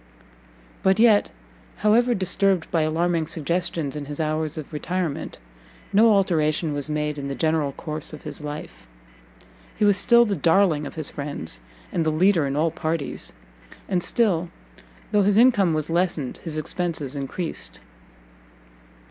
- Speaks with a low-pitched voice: No, medium, 160 Hz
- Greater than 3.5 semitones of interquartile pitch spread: Yes, average, 4.0 semitones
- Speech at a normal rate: Yes, average, 150 wpm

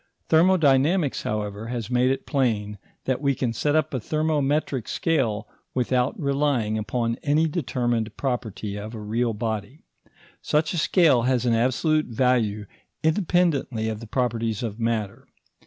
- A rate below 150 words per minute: Yes, average, 140 wpm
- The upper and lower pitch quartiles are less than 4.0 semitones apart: No, average, 4.7 semitones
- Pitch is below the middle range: Yes, low, 125 Hz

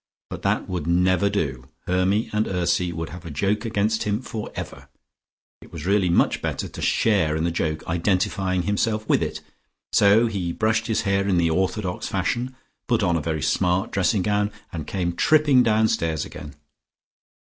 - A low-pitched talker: Yes, very low, 95 Hz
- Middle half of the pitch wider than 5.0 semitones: No, average, 3.9 semitones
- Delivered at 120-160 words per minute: No, average, 170 wpm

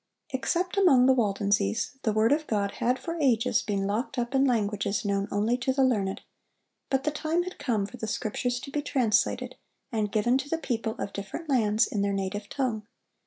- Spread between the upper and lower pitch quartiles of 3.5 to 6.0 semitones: Yes, average, 4.6 semitones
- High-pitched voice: Yes, high, 235 Hz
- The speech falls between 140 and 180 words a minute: No, average, 200 wpm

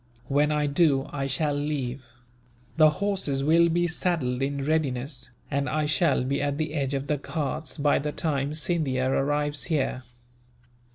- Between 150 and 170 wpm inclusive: Yes, average, 160 wpm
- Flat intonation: Yes, narrow, 2.2 semitones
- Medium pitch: Yes, medium, 145 Hz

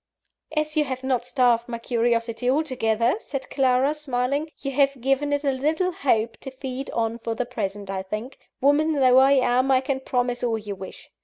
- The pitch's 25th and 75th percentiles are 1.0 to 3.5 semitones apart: Yes, average, 3.0 semitones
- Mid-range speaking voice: No, very high, 255 Hz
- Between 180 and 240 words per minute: Yes, average, 190 wpm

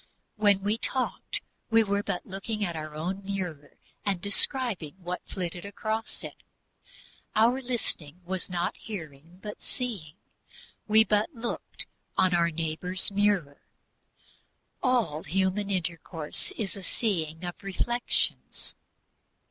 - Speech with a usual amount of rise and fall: Yes, average, 3.8 semitones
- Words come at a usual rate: No, slow, 120 wpm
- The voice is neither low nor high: No, high, 195 Hz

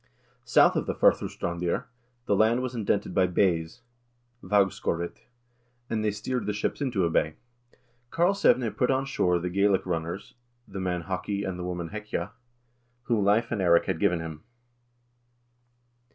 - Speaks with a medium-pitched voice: No, low, 100 Hz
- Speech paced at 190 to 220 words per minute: No, average, 160 wpm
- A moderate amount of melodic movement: Yes, average, 4.1 semitones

